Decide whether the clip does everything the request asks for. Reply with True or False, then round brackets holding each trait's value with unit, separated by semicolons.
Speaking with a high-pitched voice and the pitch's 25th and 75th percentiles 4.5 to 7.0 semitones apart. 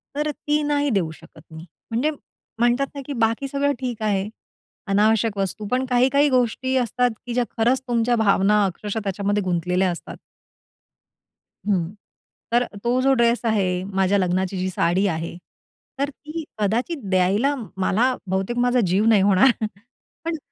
True (225 Hz; 5.0 semitones)